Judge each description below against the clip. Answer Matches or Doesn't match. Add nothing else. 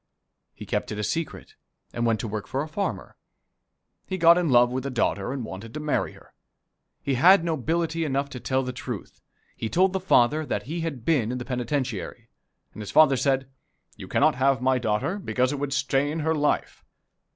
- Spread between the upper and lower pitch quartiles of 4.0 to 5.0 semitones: Matches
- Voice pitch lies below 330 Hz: Matches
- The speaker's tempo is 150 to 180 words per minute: Doesn't match